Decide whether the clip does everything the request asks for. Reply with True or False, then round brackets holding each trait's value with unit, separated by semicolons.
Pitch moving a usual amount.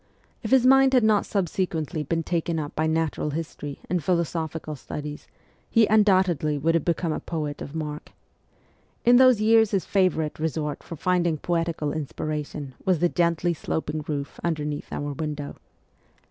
True (3.3 semitones)